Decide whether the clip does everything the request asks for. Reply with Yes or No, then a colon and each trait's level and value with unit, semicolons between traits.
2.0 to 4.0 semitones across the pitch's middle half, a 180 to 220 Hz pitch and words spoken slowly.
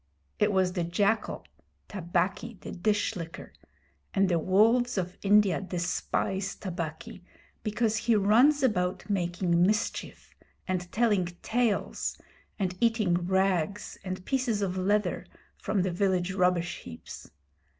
Yes: average, 2.9 semitones; high, 190 Hz; slow, 120 wpm